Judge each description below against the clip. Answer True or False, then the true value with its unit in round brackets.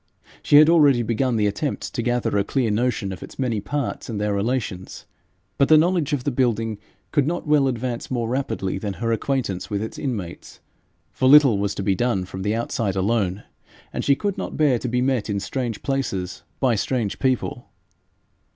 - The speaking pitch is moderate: False (120 Hz)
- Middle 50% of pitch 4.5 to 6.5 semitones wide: True (4.8 semitones)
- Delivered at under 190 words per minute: False (195 wpm)